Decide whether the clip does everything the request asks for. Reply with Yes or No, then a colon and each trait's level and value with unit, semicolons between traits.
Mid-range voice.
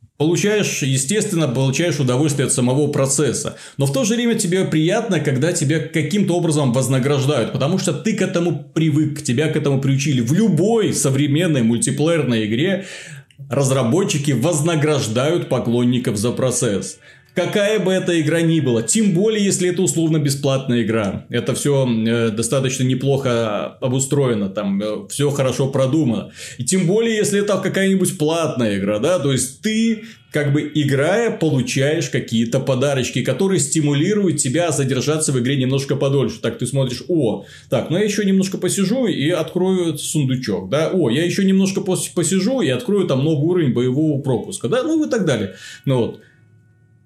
Yes: medium, 150 Hz